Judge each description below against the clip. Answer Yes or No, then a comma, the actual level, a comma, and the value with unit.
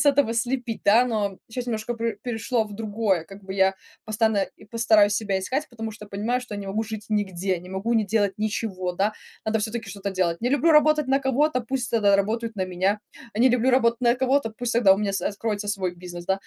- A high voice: Yes, high, 220 Hz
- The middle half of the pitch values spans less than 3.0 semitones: No, average, 3.3 semitones